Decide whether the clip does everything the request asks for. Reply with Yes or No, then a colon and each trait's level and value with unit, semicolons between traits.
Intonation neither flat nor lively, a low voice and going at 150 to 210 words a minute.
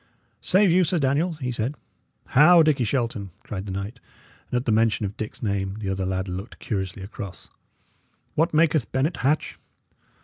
No: wide, 7.4 semitones; low, 120 Hz; average, 170 wpm